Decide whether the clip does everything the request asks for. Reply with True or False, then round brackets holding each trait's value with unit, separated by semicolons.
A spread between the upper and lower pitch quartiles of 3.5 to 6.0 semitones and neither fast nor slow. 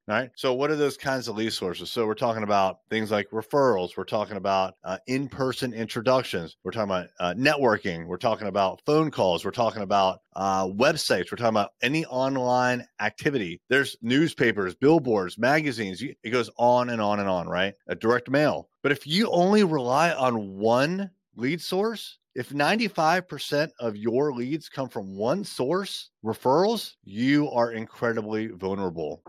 True (5.3 semitones; 165 wpm)